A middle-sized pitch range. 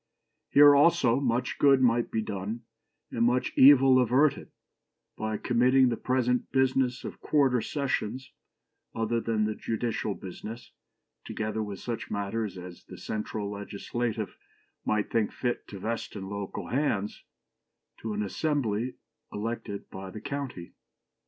Yes: average, 3.5 semitones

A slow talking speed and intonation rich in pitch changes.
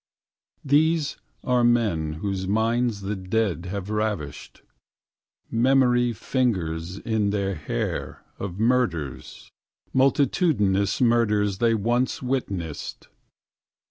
No: slow, 90 wpm; average, 4.3 semitones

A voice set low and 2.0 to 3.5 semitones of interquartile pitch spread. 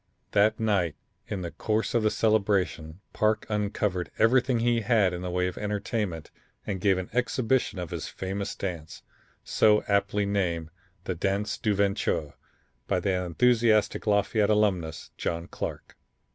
Yes: low, 100 Hz; average, 3.0 semitones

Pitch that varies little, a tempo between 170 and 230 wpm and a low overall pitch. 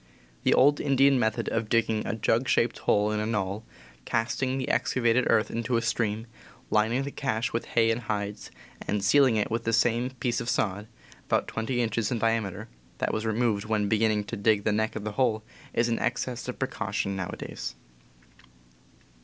Yes: narrow, 2.0 semitones; average, 185 wpm; low, 115 Hz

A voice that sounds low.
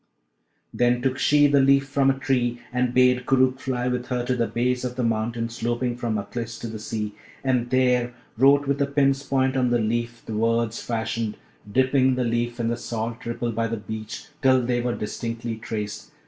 Yes: low, 120 Hz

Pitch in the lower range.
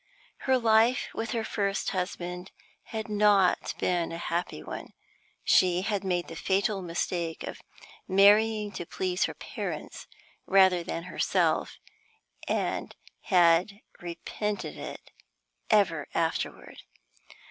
No: high, 190 Hz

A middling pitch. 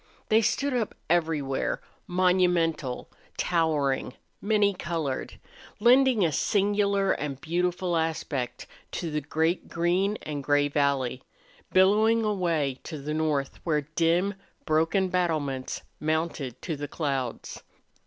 Yes: medium, 165 Hz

